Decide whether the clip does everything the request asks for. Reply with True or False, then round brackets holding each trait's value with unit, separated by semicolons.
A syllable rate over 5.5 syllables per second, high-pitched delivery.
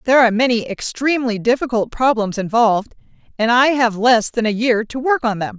True (5.8 syllables/s; 235 Hz)